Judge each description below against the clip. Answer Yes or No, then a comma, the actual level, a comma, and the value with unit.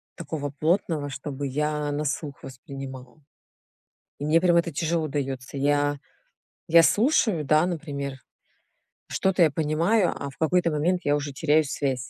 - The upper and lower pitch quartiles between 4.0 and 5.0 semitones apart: No, average, 2.9 semitones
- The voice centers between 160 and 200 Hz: No, medium, 150 Hz